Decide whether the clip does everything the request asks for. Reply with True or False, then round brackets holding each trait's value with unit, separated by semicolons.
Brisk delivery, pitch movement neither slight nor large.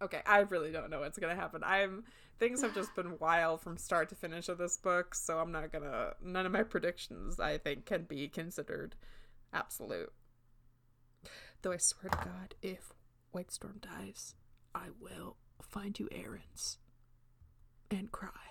False (165 wpm; 3.8 semitones)